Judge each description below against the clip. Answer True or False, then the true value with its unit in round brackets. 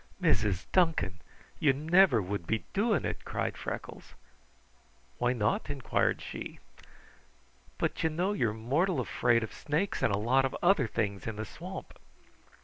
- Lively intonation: True (7.5 semitones)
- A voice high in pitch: False (130 Hz)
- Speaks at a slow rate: False (145 wpm)